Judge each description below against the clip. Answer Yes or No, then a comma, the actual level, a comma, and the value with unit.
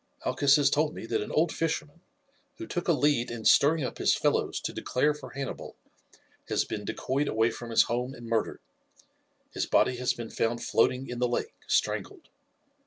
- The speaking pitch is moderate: No, low, 130 Hz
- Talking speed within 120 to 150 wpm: No, average, 185 wpm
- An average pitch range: Yes, average, 4.0 semitones